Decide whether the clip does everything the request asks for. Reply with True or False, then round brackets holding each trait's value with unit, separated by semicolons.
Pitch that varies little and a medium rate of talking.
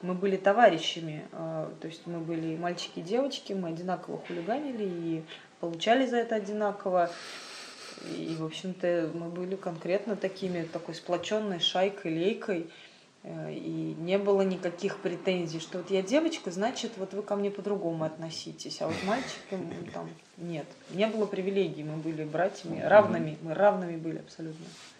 False (3.4 semitones; 145 wpm)